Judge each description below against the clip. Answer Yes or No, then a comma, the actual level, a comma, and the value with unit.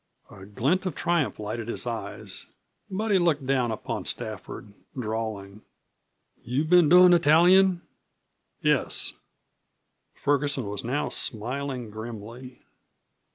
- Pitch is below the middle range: Yes, low, 130 Hz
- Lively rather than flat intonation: Yes, wide, 7.2 semitones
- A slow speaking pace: Yes, slow, 110 wpm